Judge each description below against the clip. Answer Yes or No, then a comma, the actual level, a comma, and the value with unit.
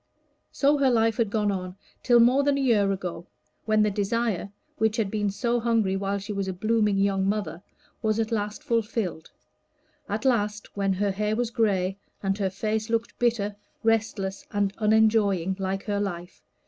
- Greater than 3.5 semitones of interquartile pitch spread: No, narrow, 2.6 semitones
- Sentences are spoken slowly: No, average, 175 wpm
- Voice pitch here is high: Yes, high, 210 Hz